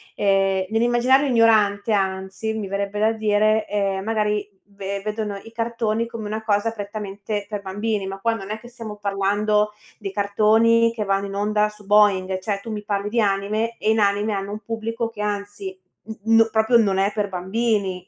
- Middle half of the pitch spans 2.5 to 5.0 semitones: No, narrow, 1.9 semitones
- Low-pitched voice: No, high, 210 Hz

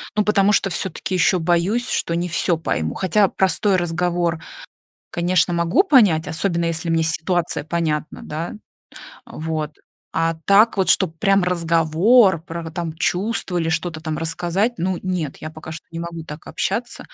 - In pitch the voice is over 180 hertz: No, medium, 170 Hz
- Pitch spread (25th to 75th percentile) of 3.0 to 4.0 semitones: No, narrow, 2.5 semitones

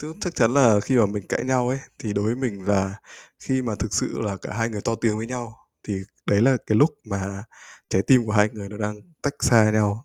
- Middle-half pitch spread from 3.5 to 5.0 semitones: No, average, 3.1 semitones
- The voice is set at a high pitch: No, low, 110 Hz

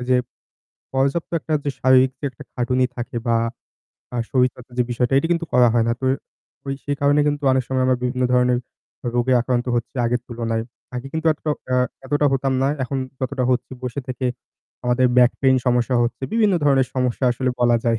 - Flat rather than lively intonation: Yes, narrow, 1.7 semitones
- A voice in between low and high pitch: No, low, 125 Hz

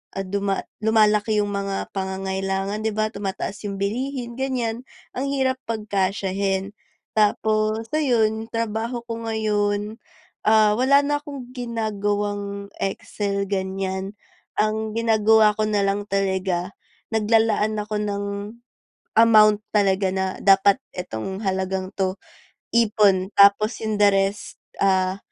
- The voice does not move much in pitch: Yes, narrow, 2.1 semitones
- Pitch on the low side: No, high, 210 Hz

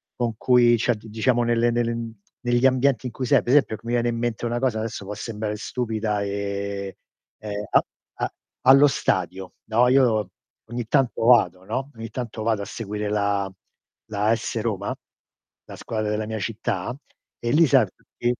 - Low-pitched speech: Yes, low, 115 Hz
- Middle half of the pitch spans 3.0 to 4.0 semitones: No, narrow, 2.5 semitones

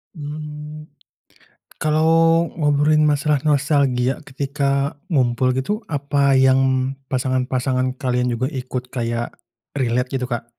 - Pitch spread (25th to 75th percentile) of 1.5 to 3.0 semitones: Yes, average, 2.7 semitones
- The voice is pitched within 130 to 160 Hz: Yes, low, 135 Hz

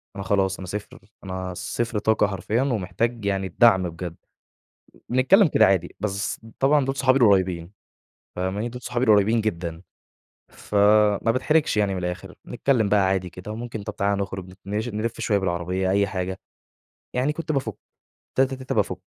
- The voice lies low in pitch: Yes, low, 100 Hz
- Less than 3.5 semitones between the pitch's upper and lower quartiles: No, average, 4.0 semitones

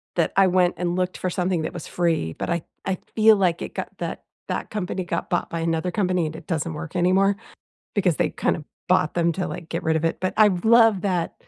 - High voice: No, medium, 180 Hz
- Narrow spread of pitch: Yes, narrow, 2.2 semitones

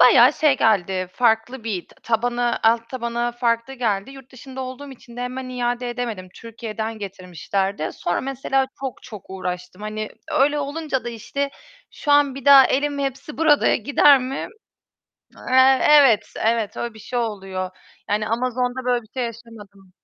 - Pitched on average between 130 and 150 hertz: No, high, 240 Hz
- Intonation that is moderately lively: Yes, average, 3.6 semitones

